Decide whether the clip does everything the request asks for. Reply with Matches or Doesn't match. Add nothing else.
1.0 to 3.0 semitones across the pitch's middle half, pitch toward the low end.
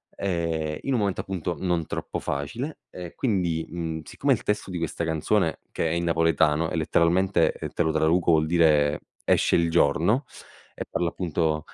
Matches